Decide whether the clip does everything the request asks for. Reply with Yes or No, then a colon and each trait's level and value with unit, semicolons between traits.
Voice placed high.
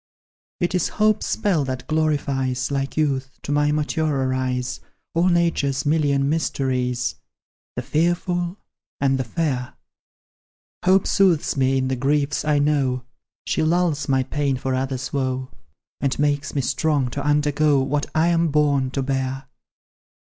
No: medium, 140 Hz